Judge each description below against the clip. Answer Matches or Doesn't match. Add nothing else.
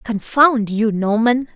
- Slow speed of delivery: Matches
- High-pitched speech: Matches